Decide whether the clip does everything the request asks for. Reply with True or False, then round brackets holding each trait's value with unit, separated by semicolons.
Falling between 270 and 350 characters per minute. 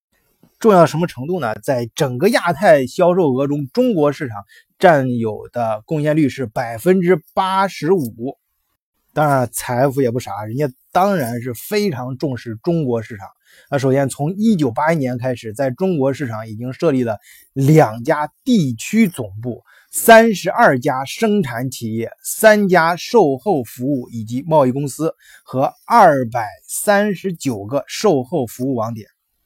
False (230 characters per minute)